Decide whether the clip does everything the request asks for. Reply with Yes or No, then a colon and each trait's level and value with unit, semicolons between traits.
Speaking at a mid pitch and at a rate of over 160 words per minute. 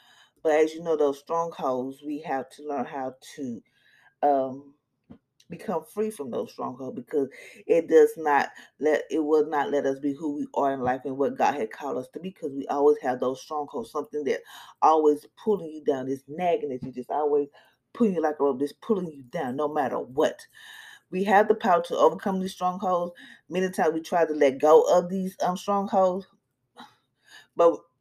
Yes: medium, 155 Hz; average, 195 wpm